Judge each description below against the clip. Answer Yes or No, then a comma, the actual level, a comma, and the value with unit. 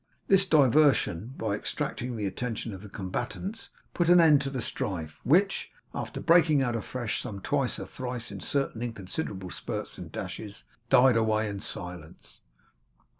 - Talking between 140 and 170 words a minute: Yes, average, 155 wpm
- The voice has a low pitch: Yes, low, 120 Hz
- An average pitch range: No, wide, 6.0 semitones